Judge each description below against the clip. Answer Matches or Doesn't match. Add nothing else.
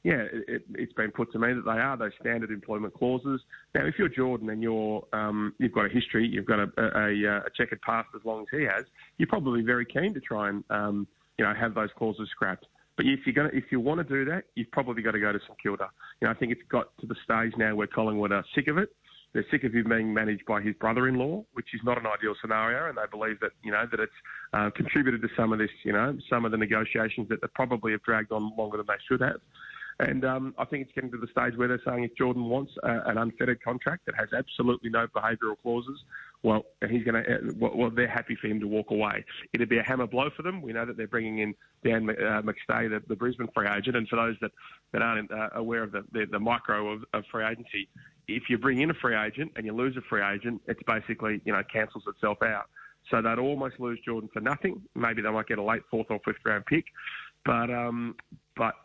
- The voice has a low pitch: Matches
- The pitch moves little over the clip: Matches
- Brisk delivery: Matches